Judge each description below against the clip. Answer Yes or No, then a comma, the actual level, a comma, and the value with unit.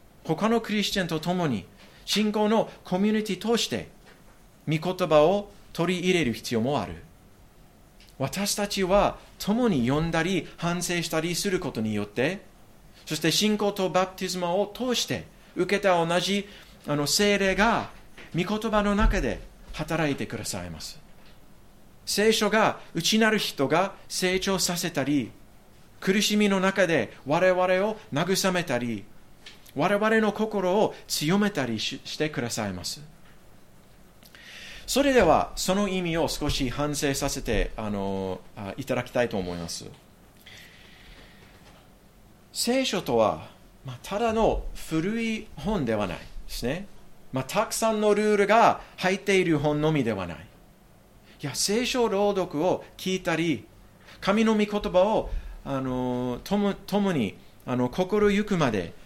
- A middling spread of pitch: No, wide, 6.6 semitones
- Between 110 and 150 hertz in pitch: No, medium, 180 Hz